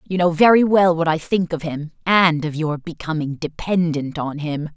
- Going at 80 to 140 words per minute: No, average, 200 wpm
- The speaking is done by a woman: Yes, female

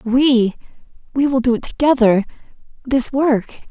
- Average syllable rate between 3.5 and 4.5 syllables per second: Yes, 4.2 syllables/s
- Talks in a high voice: Yes, very high, 250 Hz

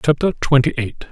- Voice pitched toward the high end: No, low, 130 Hz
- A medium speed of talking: Yes, average, 160 wpm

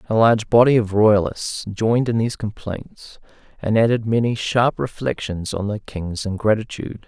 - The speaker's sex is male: Yes, male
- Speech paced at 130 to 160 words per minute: Yes, average, 155 wpm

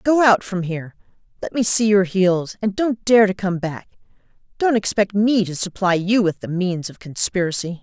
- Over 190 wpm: Yes, average, 200 wpm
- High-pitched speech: Yes, high, 195 Hz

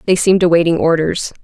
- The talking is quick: No, average, 165 wpm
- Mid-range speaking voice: Yes, medium, 170 Hz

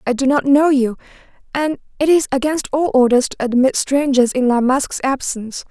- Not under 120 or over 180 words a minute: No, average, 190 wpm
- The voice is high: Yes, very high, 265 Hz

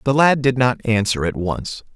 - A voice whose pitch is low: Yes, low, 120 Hz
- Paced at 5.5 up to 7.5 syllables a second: No, 4.6 syllables/s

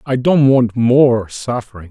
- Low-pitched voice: Yes, low, 125 Hz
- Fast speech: No, average, 160 wpm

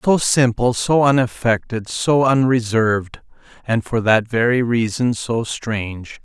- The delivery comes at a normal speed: No, slow, 125 wpm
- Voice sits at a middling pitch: No, low, 120 Hz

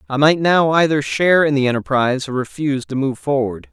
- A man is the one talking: Yes, male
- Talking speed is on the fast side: Yes, fast, 210 wpm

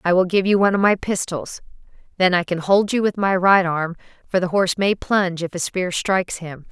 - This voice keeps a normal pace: No, fast, 240 wpm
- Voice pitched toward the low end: No, medium, 185 Hz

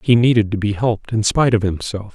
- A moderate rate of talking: No, fast, 250 wpm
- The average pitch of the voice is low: Yes, low, 110 Hz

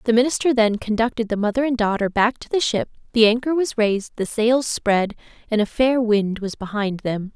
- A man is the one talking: No, female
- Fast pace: Yes, fast, 210 wpm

